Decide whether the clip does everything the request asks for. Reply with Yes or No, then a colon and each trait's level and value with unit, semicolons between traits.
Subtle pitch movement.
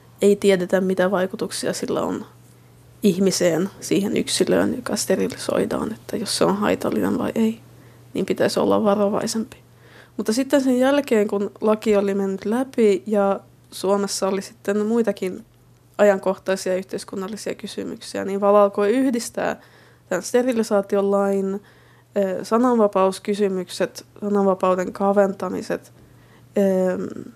Yes: narrow, 1.9 semitones